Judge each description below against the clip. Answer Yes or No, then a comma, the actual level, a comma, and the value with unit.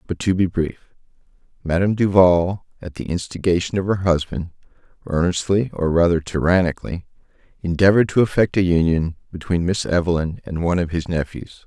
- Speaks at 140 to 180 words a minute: Yes, average, 150 wpm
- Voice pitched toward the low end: Yes, very low, 90 Hz